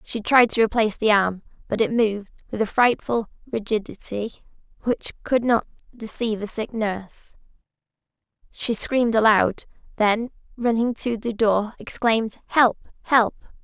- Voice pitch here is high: Yes, high, 220 Hz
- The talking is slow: Yes, slow, 130 wpm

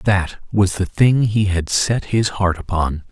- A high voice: No, very low, 95 Hz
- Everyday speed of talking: Yes, average, 195 wpm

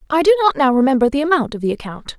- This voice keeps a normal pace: No, fast, 275 wpm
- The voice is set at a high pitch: Yes, very high, 285 Hz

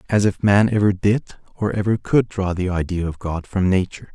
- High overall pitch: No, low, 100 Hz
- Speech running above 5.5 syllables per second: No, 5.3 syllables/s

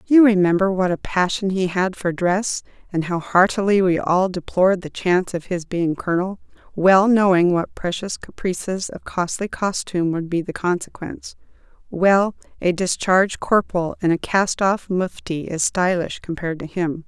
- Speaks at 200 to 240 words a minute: No, average, 165 wpm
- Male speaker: No, female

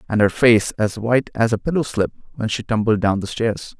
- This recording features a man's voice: Yes, male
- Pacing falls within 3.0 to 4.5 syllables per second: No, 5.5 syllables/s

